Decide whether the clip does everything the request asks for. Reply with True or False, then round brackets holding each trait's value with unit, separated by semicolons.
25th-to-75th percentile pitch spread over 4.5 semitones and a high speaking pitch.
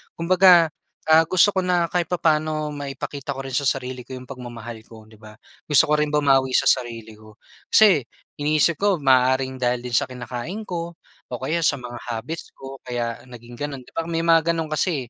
False (4.9 semitones; 140 Hz)